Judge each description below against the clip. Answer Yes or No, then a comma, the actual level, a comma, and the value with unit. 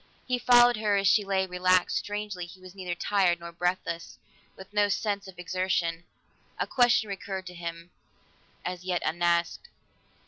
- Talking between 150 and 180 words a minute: Yes, average, 160 wpm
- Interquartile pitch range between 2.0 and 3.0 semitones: Yes, narrow, 2.6 semitones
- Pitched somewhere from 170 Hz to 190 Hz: Yes, medium, 185 Hz